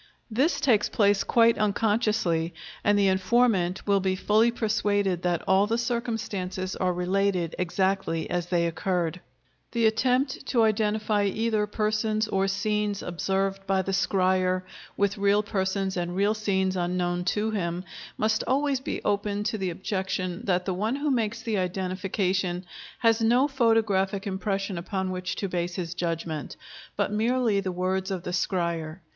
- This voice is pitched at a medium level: No, high, 195 Hz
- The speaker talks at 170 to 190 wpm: No, average, 150 wpm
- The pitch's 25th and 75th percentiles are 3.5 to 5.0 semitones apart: No, average, 2.8 semitones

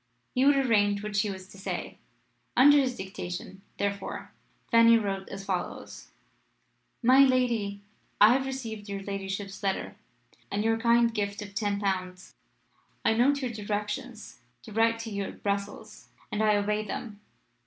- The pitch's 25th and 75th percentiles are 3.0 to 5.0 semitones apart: No, narrow, 2.6 semitones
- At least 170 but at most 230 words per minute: No, average, 155 wpm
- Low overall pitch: No, high, 210 Hz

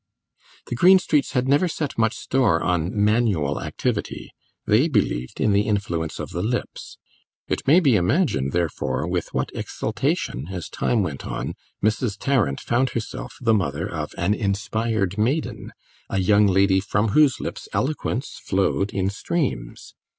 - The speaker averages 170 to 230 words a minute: No, average, 150 wpm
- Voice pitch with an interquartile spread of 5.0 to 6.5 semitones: Yes, wide, 5.6 semitones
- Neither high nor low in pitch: No, low, 105 Hz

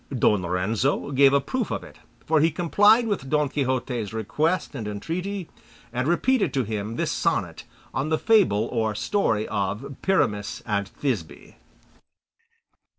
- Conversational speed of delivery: Yes, average, 145 wpm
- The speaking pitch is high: No, low, 135 Hz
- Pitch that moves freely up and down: Yes, wide, 7.5 semitones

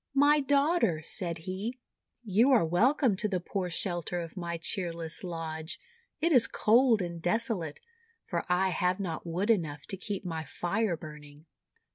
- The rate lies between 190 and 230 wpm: No, average, 155 wpm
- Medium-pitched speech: Yes, medium, 180 Hz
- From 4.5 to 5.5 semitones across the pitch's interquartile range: Yes, average, 5.1 semitones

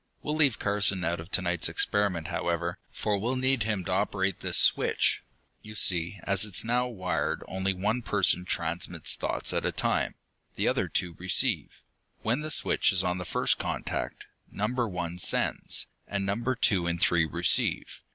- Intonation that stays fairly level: No, average, 3.6 semitones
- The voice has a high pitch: No, very low, 95 Hz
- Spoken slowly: No, average, 175 wpm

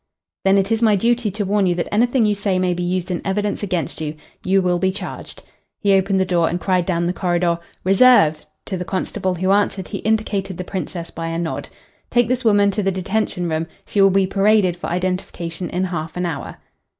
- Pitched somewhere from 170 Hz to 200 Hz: Yes, high, 190 Hz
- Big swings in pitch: No, narrow, 2.5 semitones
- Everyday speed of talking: No, fast, 220 wpm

